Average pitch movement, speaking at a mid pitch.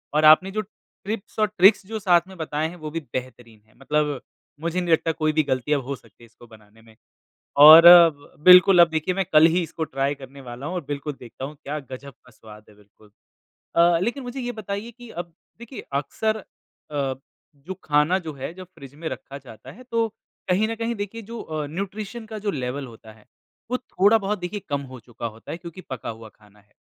No: wide, 6.8 semitones; medium, 155 Hz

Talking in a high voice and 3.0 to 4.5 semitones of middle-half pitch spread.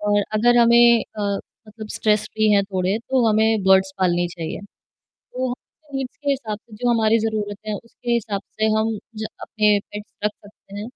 No: high, 215 Hz; narrow, 2.4 semitones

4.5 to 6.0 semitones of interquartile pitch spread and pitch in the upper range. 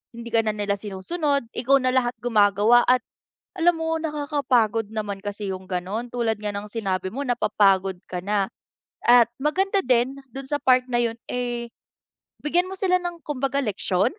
Yes: average, 5.0 semitones; high, 240 Hz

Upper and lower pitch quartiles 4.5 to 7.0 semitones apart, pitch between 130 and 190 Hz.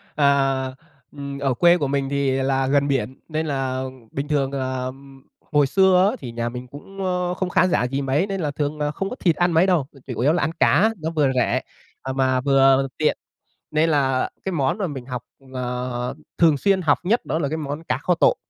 No: average, 3.6 semitones; medium, 140 Hz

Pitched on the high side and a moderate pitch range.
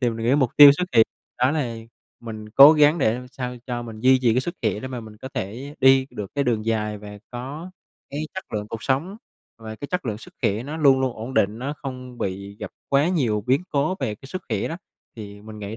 No: low, 125 Hz; average, 4.3 semitones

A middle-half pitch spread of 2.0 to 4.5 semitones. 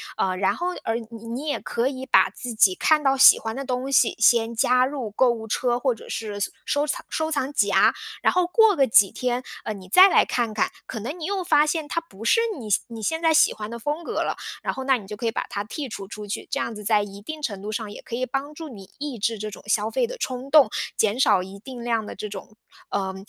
No: average, 5.1 semitones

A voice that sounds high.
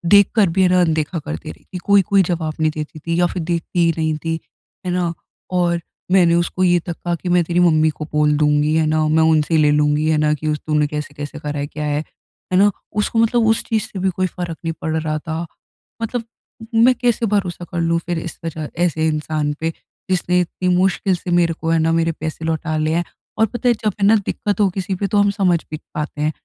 No: medium, 165 Hz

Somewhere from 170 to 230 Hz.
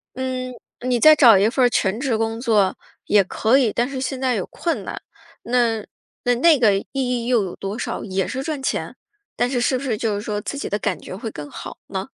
No: high, 240 Hz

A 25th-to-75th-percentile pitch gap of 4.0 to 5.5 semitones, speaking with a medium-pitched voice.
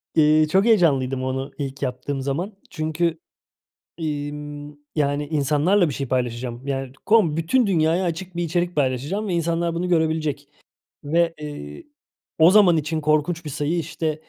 No: average, 3.2 semitones; medium, 155 Hz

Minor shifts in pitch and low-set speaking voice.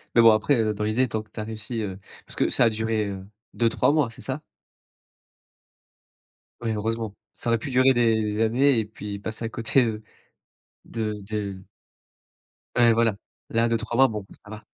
Yes: narrow, 1.6 semitones; low, 110 Hz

